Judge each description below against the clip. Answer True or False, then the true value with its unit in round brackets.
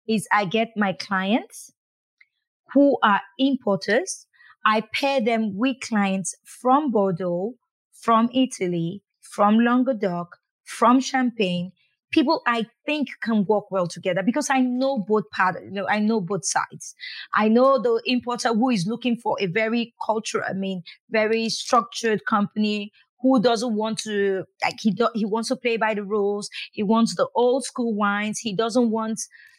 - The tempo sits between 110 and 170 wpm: True (160 wpm)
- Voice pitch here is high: True (225 Hz)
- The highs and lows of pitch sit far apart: False (3.5 semitones)